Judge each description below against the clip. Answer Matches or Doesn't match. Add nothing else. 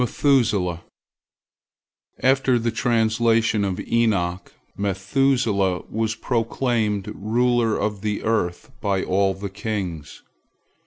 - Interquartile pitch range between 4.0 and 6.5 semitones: Doesn't match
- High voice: Doesn't match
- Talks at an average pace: Doesn't match